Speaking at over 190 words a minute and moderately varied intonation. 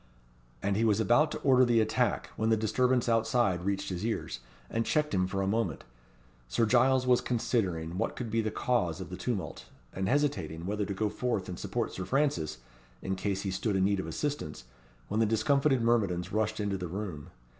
Yes: average, 200 wpm; average, 4.1 semitones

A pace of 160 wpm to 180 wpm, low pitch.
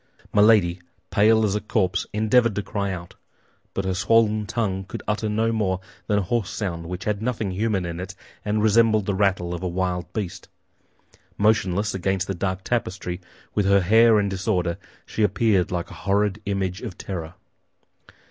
Yes: average, 175 wpm; low, 100 Hz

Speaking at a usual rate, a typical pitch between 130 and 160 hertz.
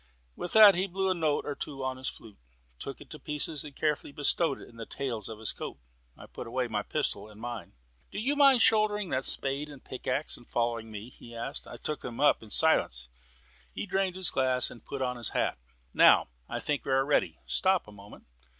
No: fast, 225 wpm; low, 135 Hz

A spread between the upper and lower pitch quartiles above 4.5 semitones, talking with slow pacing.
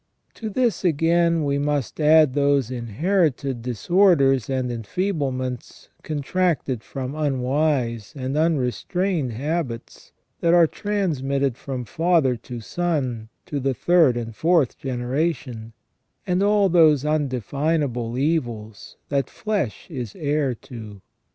Yes: average, 4.9 semitones; slow, 120 wpm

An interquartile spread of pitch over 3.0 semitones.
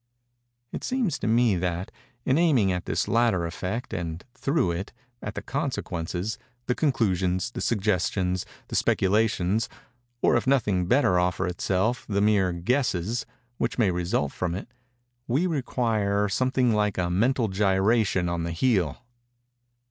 Yes: average, 5.0 semitones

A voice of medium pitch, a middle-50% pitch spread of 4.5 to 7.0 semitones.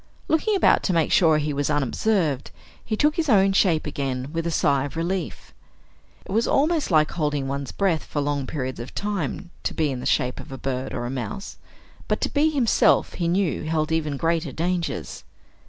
Yes: medium, 160 Hz; wide, 5.6 semitones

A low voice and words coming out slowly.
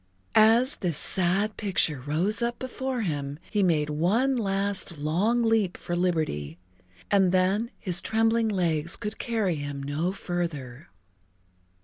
No: medium, 185 Hz; slow, 130 wpm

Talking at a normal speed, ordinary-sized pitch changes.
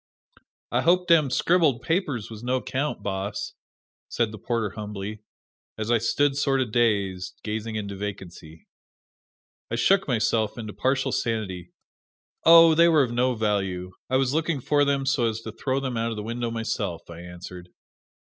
Yes: average, 165 wpm; average, 4.7 semitones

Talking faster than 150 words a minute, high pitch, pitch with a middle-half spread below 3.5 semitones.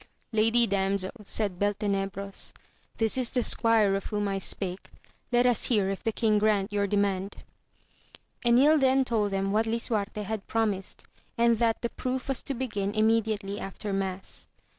Yes: average, 160 wpm; high, 210 Hz; average, 2.7 semitones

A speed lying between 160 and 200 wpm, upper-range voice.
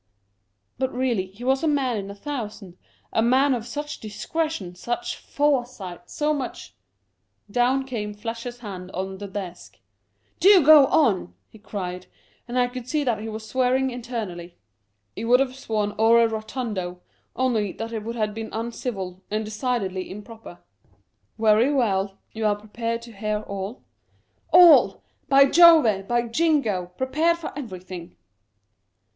Yes: average, 165 wpm; high, 225 Hz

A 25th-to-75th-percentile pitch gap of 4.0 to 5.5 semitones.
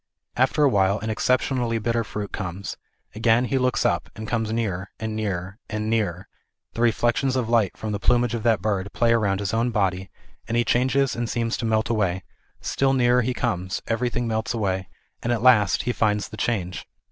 No: average, 2.8 semitones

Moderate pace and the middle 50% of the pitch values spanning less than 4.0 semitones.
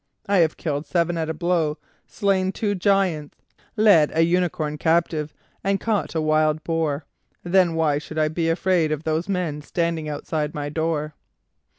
Yes: average, 165 wpm; average, 2.7 semitones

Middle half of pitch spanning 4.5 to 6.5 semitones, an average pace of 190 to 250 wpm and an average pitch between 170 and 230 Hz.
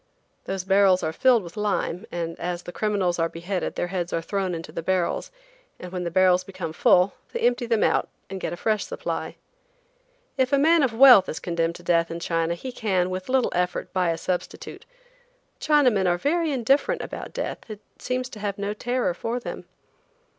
Yes: average, 5.1 semitones; average, 195 wpm; high, 190 Hz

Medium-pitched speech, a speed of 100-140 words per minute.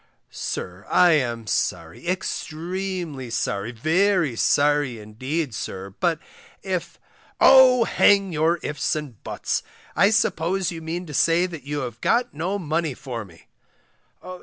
Yes: medium, 160 Hz; slow, 135 wpm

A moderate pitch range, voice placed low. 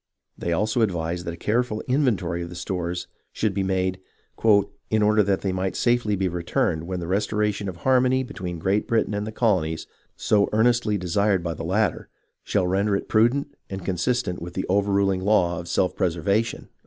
Yes: average, 3.4 semitones; low, 100 Hz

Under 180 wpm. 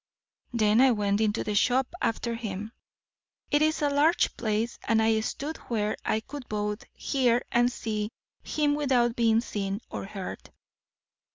Yes: average, 155 wpm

